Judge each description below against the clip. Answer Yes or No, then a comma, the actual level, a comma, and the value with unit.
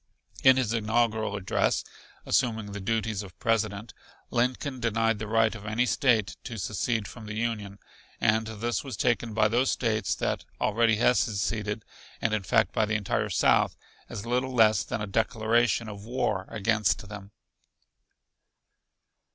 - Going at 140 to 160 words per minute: Yes, average, 150 wpm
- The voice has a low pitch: Yes, low, 110 Hz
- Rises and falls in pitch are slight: Yes, narrow, 1.9 semitones